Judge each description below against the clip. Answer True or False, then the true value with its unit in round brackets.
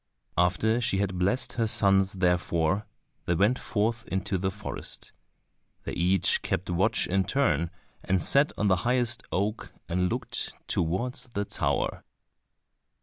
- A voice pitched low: True (95 Hz)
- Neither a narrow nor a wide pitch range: True (3.7 semitones)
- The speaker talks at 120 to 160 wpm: True (140 wpm)